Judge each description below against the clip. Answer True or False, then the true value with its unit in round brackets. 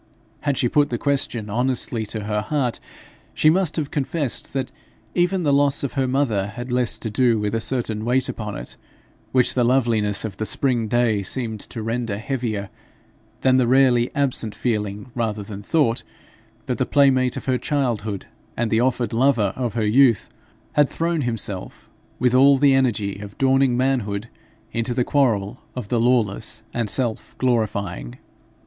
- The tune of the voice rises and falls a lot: False (3.6 semitones)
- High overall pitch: False (120 Hz)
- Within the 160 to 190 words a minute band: True (170 wpm)